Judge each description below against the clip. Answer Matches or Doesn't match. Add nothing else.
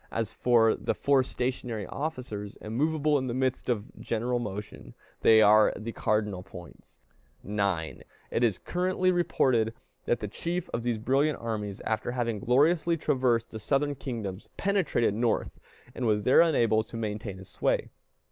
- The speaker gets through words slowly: Doesn't match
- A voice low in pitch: Matches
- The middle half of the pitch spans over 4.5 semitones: Doesn't match